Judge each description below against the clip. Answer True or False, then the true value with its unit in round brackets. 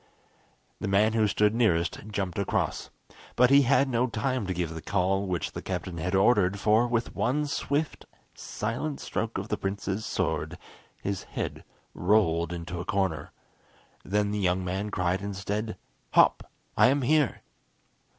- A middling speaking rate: True (155 wpm)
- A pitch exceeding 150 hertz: False (100 Hz)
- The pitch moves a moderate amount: True (4.0 semitones)